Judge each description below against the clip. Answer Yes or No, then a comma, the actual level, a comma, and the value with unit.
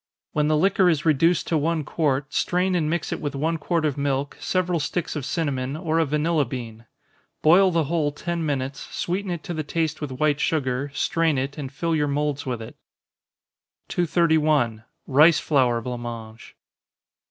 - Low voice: No, medium, 150 Hz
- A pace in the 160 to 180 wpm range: Yes, average, 175 wpm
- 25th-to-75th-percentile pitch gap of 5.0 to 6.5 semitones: No, average, 3.4 semitones